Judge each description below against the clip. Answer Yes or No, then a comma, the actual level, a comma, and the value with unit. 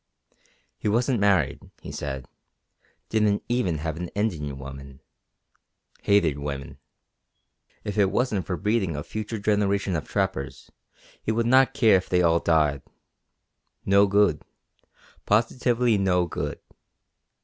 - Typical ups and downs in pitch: No, wide, 5.7 semitones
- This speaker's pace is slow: Yes, slow, 125 wpm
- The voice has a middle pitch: No, very low, 95 Hz